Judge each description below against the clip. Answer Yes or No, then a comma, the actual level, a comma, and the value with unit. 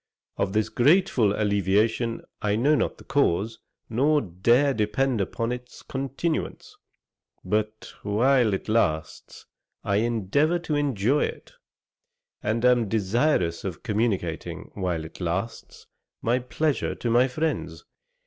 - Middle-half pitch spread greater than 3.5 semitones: Yes, average, 4.8 semitones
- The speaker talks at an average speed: No, slow, 120 wpm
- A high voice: No, low, 115 Hz